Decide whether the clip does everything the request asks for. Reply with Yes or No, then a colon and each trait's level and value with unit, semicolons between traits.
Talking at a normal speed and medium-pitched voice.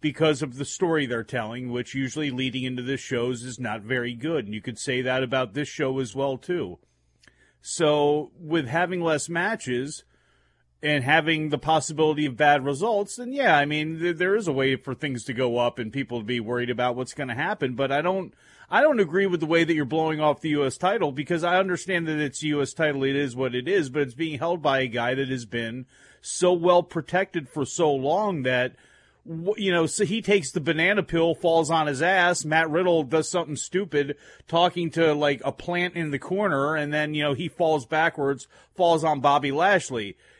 No: fast, 215 wpm; medium, 150 Hz